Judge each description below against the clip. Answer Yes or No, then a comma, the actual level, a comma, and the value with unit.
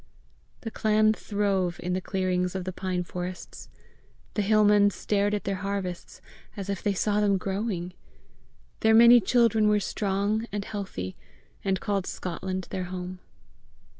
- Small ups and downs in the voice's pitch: Yes, narrow, 2.2 semitones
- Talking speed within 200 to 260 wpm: No, average, 150 wpm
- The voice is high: Yes, high, 195 Hz